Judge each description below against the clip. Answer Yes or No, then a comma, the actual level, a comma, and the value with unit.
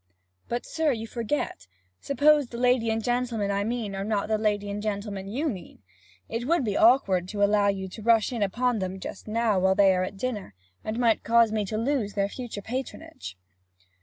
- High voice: Yes, high, 215 Hz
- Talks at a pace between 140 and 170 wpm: No, average, 200 wpm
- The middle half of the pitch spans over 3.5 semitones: No, average, 3.2 semitones